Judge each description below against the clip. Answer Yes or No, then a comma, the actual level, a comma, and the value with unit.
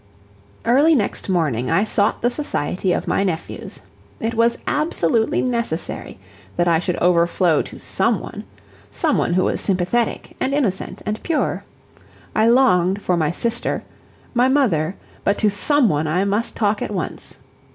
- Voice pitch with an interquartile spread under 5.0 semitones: No, average, 5.3 semitones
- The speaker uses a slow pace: No, average, 155 wpm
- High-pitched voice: Yes, high, 200 Hz